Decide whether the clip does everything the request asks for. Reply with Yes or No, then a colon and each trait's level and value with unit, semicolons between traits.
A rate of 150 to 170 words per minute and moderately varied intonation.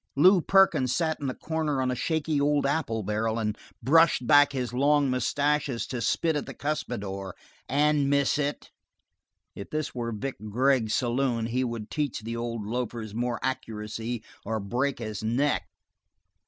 Yes: average, 160 wpm; average, 4.1 semitones